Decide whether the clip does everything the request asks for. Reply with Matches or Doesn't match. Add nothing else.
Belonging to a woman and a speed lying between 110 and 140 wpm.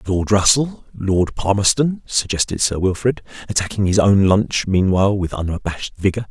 Doesn't match